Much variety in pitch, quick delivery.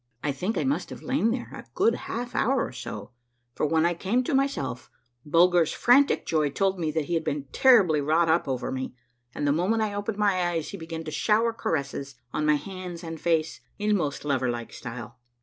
Yes: wide, 6.1 semitones; fast, 215 wpm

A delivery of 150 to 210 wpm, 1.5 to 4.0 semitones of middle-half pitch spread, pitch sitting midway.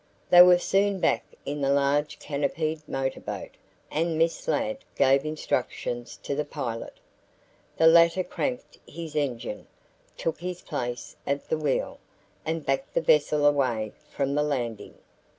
No: average, 140 wpm; average, 3.3 semitones; medium, 150 Hz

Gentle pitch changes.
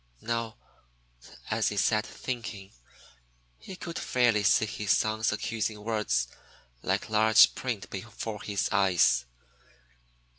Yes: narrow, 1.9 semitones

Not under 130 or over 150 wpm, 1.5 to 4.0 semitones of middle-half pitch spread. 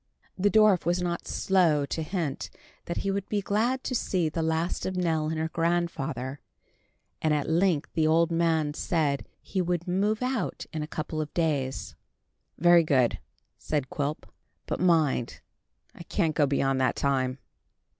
No: average, 165 wpm; average, 3.3 semitones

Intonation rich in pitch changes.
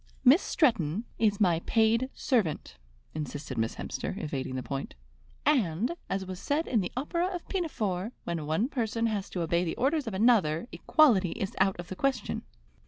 Yes: wide, 6.8 semitones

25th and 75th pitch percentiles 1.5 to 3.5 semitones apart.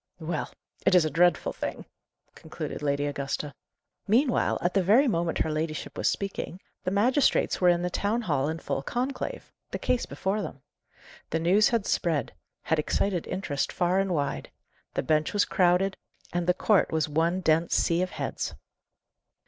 No: average, 4.0 semitones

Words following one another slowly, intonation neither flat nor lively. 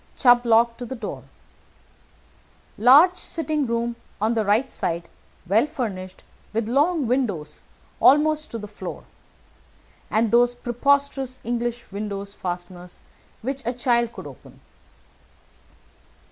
Yes: slow, 120 wpm; average, 4.0 semitones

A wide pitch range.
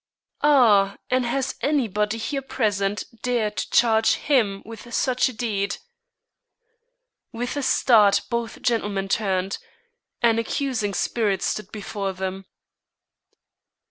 No: average, 3.7 semitones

